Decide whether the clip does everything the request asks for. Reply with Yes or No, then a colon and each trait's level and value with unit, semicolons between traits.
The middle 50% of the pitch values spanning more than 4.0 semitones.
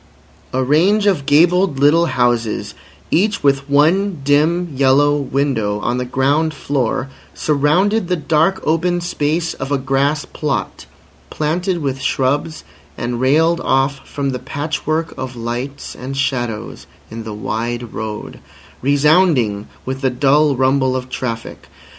No: average, 3.6 semitones